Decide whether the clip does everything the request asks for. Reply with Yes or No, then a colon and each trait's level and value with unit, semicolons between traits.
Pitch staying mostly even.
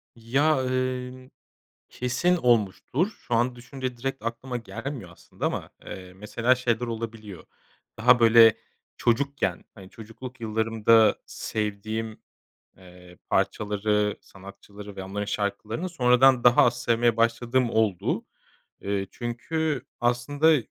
No: average, 3.1 semitones